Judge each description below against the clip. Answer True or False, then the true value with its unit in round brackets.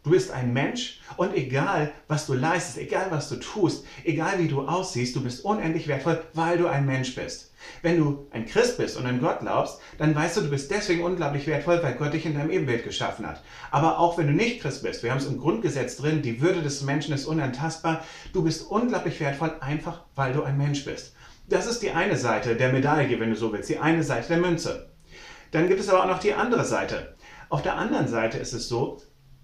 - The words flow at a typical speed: False (230 wpm)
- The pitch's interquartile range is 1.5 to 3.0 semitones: False (3.6 semitones)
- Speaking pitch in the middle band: True (155 Hz)